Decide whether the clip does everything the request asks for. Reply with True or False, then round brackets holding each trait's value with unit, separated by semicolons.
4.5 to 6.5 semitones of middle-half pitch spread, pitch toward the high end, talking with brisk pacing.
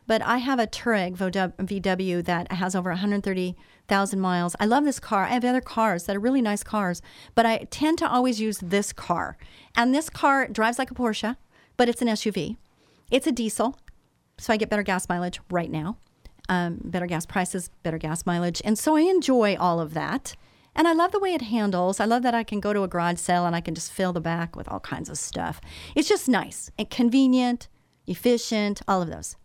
True (5.2 semitones; 210 Hz; 215 wpm)